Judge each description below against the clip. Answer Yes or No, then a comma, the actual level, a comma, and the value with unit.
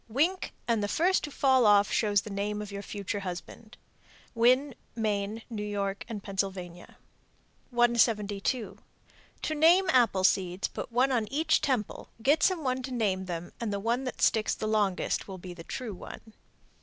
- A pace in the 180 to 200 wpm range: No, average, 170 wpm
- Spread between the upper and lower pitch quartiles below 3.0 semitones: No, average, 4.1 semitones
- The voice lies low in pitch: No, high, 215 Hz